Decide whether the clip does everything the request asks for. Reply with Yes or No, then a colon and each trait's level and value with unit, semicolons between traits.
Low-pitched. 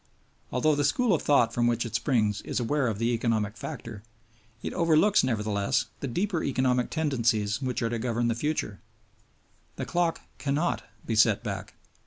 Yes: low, 120 Hz